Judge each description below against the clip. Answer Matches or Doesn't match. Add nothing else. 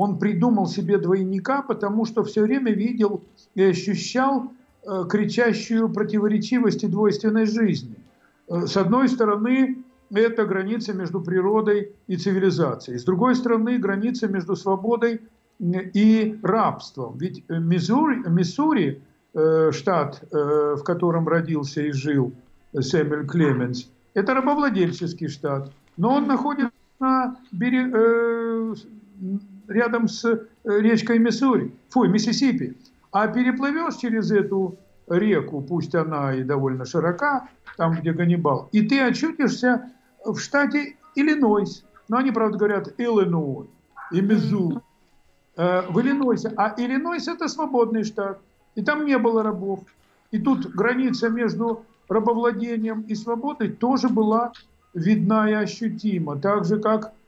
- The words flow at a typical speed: Matches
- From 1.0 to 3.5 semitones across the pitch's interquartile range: Doesn't match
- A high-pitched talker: Matches